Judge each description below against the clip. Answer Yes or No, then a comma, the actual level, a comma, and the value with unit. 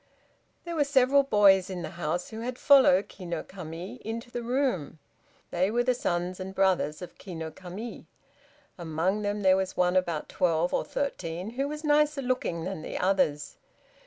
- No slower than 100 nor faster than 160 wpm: No, average, 180 wpm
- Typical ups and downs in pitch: No, wide, 5.8 semitones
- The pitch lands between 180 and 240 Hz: Yes, high, 190 Hz